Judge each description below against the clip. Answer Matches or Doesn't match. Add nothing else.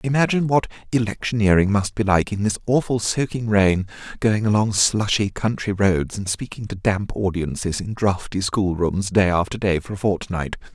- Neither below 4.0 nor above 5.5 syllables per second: Matches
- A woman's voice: Doesn't match